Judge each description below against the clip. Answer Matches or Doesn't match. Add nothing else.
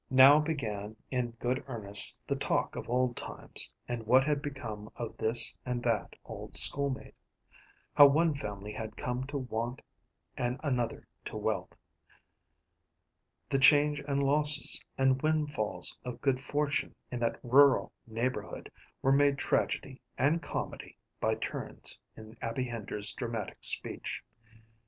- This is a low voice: Matches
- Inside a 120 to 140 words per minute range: Matches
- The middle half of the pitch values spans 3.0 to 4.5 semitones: Matches